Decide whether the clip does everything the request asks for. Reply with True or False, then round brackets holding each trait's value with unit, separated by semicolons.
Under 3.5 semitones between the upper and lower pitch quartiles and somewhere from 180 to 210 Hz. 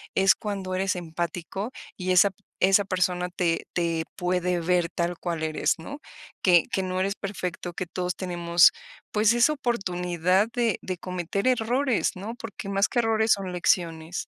True (2.4 semitones; 185 Hz)